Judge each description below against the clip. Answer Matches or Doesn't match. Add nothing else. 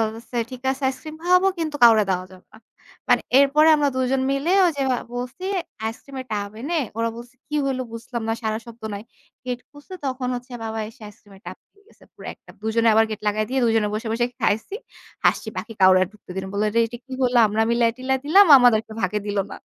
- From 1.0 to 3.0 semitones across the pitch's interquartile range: Doesn't match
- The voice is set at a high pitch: Matches